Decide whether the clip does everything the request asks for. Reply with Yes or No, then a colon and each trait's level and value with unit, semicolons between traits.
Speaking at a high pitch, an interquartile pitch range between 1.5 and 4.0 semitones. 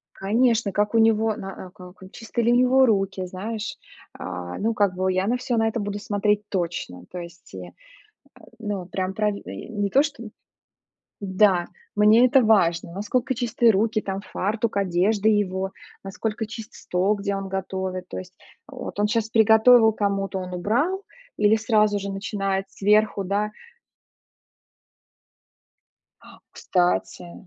Yes: high, 205 Hz; average, 2.8 semitones